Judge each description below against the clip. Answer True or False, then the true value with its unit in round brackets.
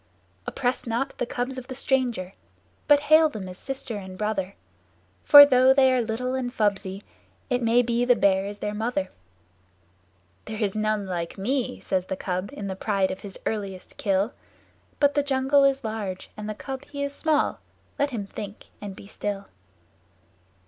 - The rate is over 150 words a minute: True (180 wpm)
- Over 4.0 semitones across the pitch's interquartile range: True (4.9 semitones)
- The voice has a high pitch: True (225 Hz)